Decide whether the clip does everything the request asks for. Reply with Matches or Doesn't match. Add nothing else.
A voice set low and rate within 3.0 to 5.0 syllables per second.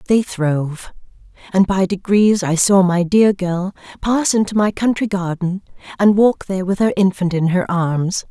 Doesn't match